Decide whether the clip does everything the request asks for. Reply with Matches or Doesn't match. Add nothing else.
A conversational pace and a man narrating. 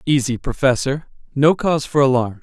Matches